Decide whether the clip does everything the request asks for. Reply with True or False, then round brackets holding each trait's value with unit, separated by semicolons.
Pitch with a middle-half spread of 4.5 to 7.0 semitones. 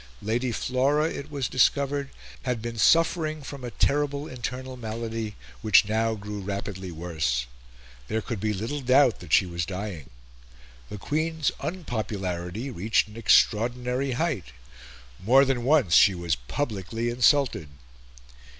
True (5.4 semitones)